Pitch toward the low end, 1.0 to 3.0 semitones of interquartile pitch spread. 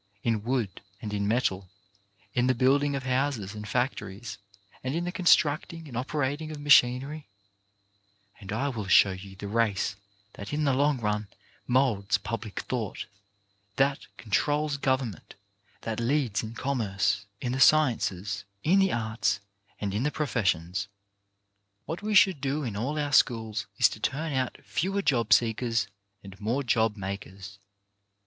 No: low, 120 Hz; wide, 5.4 semitones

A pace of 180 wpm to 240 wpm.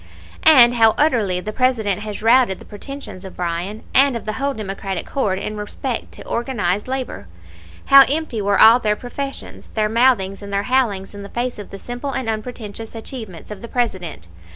Yes: average, 185 wpm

